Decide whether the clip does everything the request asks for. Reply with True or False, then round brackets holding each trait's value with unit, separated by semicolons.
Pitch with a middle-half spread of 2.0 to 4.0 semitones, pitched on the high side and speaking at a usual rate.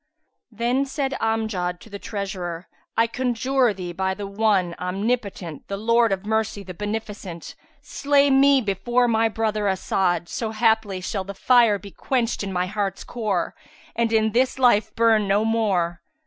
True (3.2 semitones; 215 Hz; 160 wpm)